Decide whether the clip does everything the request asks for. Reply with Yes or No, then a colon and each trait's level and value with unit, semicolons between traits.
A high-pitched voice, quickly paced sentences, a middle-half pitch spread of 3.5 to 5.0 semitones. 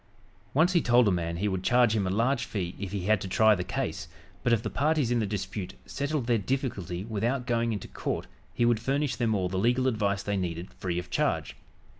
No: low, 110 Hz; fast, 230 wpm; average, 4.5 semitones